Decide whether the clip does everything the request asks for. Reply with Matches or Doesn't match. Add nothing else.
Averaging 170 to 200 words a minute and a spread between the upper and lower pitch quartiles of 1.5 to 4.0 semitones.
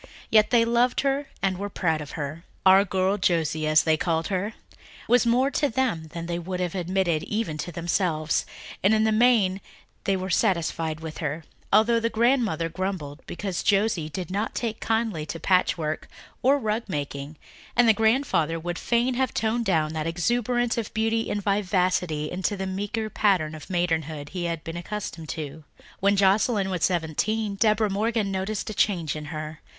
Doesn't match